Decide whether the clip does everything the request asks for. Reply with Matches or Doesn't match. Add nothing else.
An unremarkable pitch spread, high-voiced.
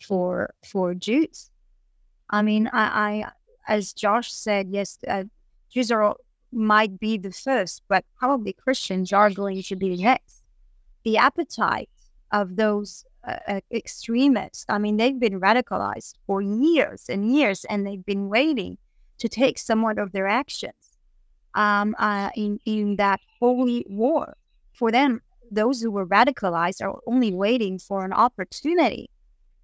Matches